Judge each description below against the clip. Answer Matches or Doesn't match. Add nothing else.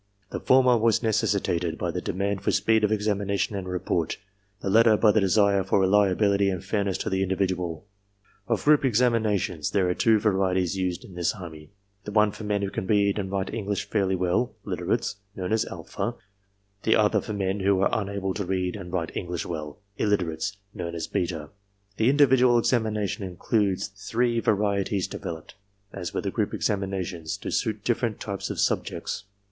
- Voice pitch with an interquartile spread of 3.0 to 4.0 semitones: Doesn't match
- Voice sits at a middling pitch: Doesn't match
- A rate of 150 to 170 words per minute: Doesn't match